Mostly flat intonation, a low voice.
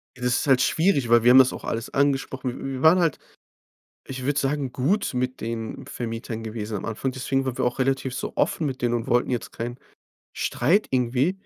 Yes: narrow, 2.1 semitones; low, 130 Hz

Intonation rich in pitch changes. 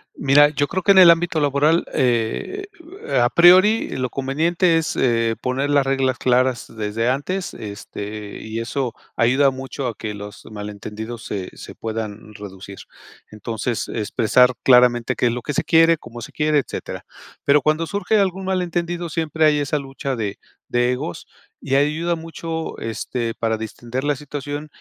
Yes: wide, 5.8 semitones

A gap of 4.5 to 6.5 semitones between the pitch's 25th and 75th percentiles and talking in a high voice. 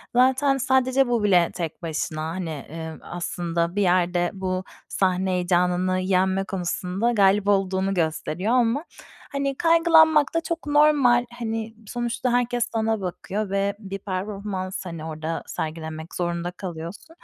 Yes: wide, 5.4 semitones; high, 195 Hz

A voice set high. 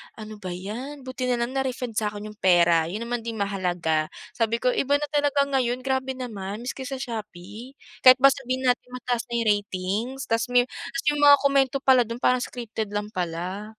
Yes: high, 235 Hz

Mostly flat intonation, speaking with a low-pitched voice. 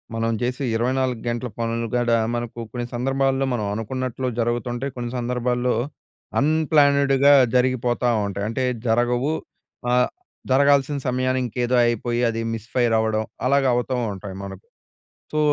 Yes: narrow, 2.0 semitones; low, 125 Hz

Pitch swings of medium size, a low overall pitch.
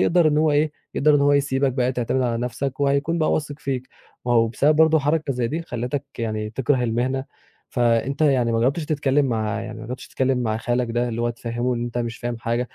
Yes: average, 3.3 semitones; low, 125 Hz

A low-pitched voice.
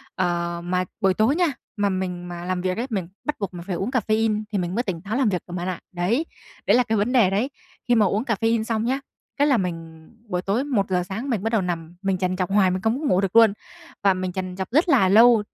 No: high, 195 Hz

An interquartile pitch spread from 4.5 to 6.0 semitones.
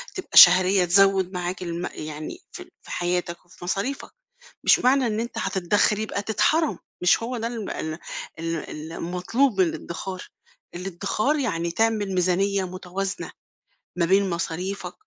No: average, 3.3 semitones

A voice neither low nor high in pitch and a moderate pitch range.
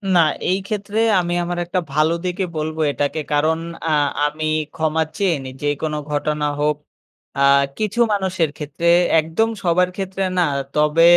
Yes: medium, 165 Hz; average, 3.4 semitones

